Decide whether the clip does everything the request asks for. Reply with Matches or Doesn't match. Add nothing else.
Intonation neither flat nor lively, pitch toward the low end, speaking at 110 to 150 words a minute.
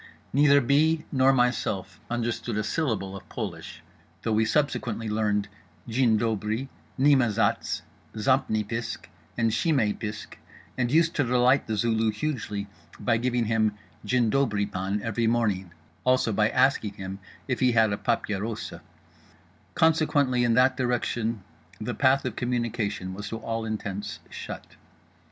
Matches